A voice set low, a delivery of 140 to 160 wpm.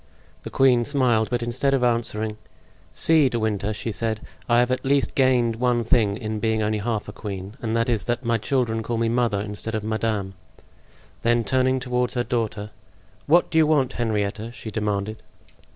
No: low, 115 Hz; average, 185 wpm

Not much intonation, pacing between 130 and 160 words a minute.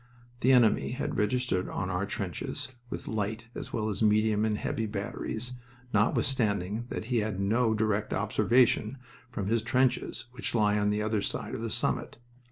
No: narrow, 2.3 semitones; average, 170 wpm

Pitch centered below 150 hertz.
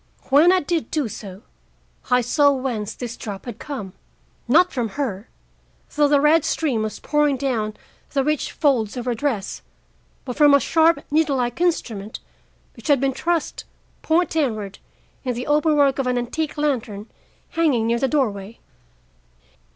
No: very high, 270 Hz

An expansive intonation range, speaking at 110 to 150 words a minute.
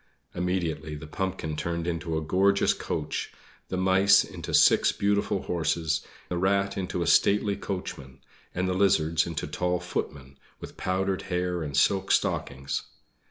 No: average, 3.2 semitones; average, 145 wpm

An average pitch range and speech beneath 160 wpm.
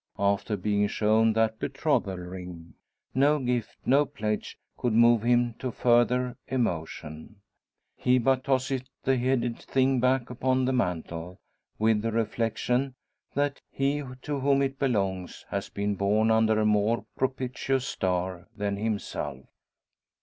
Yes: average, 4.2 semitones; slow, 135 wpm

